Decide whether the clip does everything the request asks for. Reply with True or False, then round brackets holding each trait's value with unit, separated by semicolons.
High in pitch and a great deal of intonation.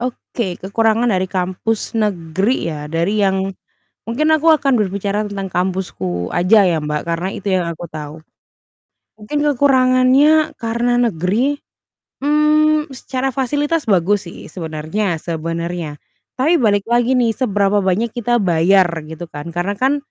True (205 Hz; 6.4 semitones)